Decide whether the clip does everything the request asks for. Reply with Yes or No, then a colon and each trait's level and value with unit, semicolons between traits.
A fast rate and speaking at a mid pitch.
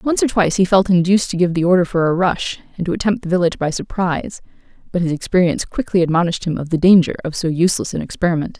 Yes: fast, 235 wpm; medium, 180 Hz